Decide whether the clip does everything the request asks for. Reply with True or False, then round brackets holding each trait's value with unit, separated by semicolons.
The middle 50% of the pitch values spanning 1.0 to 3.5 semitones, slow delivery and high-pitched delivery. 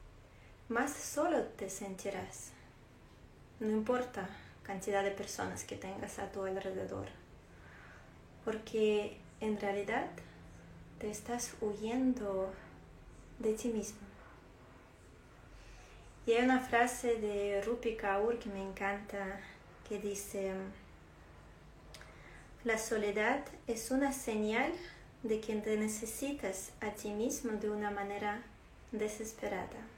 True (2.8 semitones; 100 wpm; 210 Hz)